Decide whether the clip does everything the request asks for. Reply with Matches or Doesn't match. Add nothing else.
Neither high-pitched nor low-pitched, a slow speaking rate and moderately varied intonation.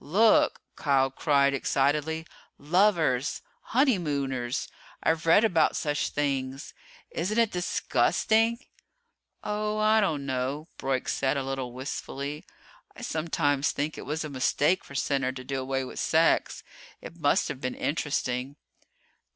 Matches